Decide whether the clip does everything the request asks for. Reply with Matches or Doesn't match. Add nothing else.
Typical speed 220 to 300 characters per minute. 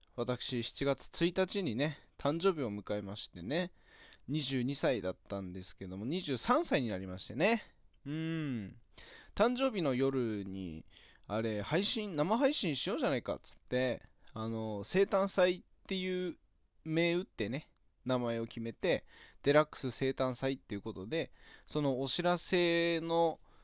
Matches